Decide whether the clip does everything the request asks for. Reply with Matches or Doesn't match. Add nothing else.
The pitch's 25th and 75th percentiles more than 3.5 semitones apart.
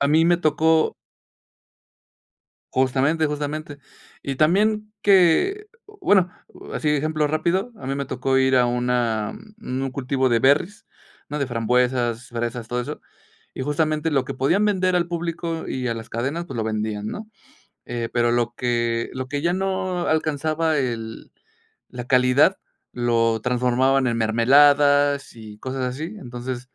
Matches